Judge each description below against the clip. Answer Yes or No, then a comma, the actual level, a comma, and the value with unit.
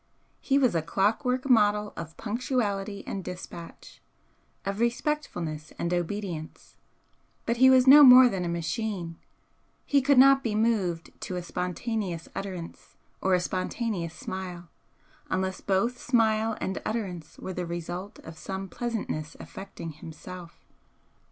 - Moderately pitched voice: No, high, 195 Hz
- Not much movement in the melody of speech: No, average, 5.0 semitones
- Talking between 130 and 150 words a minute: Yes, slow, 135 wpm